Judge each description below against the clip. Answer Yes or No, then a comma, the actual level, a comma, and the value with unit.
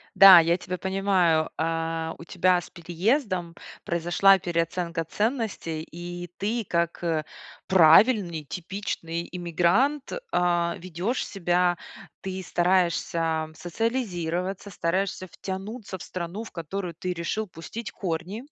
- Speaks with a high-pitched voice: No, medium, 175 Hz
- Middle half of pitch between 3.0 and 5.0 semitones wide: No, narrow, 2.6 semitones